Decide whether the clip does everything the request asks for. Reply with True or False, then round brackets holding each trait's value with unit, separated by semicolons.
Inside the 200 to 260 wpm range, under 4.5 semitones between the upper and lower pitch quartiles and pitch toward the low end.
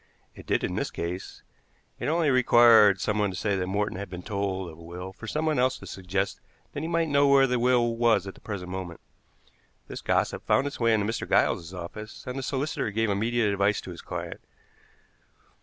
False (205 wpm; 4.9 semitones; 105 Hz)